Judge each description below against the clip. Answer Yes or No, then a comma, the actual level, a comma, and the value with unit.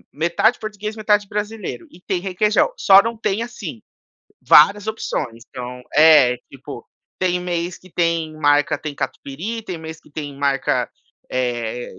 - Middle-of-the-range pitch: Yes, medium, 175 Hz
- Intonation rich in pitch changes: Yes, wide, 6.2 semitones